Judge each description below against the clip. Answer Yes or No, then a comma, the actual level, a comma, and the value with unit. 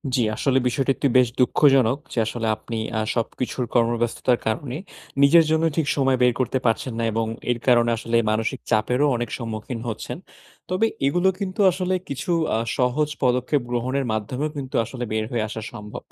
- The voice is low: Yes, low, 125 Hz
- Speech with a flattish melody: No, average, 3.2 semitones